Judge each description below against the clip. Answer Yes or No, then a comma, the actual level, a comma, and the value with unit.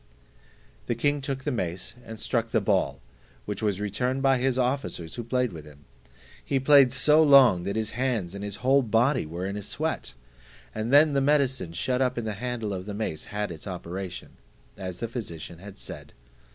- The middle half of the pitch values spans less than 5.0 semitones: No, wide, 5.5 semitones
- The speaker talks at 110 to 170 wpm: No, average, 195 wpm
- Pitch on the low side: Yes, low, 115 Hz